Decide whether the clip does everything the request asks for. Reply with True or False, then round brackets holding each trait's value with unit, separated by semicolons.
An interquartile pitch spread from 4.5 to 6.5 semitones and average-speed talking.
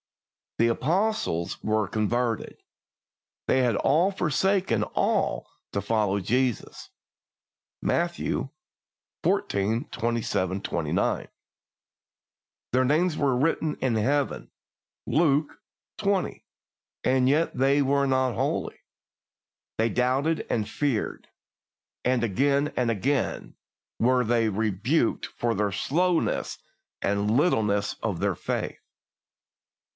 False (4.9 semitones; 100 wpm)